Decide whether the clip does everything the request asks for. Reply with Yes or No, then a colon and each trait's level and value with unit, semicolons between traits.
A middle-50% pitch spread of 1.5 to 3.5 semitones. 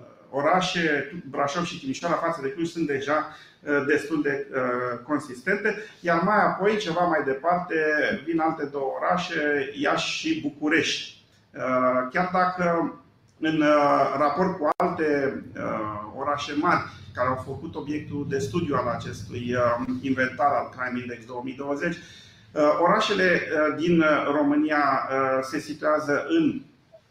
No: average, 4.1 semitones